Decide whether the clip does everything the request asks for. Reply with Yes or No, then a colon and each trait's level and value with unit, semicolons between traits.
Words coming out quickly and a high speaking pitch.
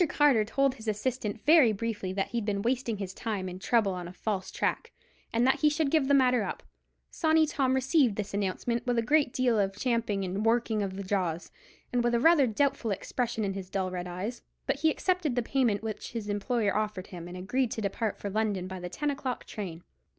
Yes: fast, 220 wpm; high, 220 Hz